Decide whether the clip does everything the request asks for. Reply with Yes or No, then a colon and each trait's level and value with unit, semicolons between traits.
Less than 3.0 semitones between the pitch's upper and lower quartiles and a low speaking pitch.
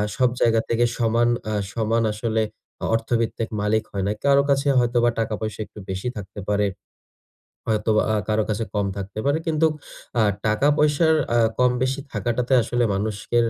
Yes: narrow, 2.5 semitones; low, 115 Hz